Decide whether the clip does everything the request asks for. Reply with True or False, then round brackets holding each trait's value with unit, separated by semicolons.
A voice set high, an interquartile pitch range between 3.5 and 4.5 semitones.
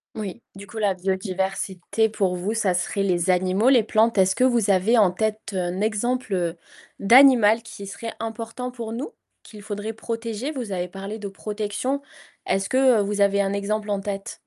False (205 Hz; 2.9 semitones)